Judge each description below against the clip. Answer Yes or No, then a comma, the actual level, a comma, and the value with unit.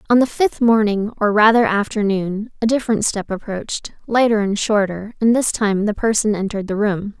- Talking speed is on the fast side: No, average, 175 wpm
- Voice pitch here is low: No, high, 210 Hz